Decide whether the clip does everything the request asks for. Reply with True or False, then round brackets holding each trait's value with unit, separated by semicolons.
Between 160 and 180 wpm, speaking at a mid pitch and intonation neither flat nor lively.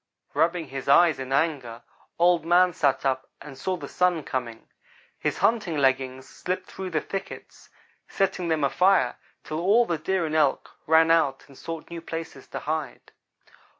True (165 wpm; 160 Hz; 4.5 semitones)